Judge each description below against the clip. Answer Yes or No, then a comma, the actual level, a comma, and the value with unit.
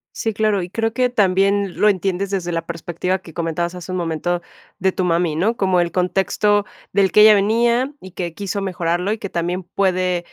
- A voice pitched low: No, medium, 185 Hz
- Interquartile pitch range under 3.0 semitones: Yes, narrow, 2.6 semitones